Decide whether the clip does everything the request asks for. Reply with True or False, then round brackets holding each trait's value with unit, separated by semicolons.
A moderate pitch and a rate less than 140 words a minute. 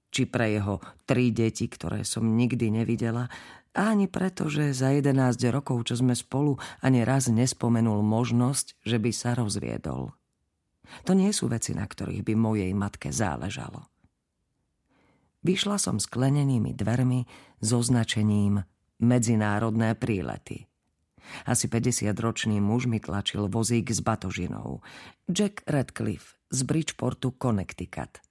False (120 Hz; 125 wpm)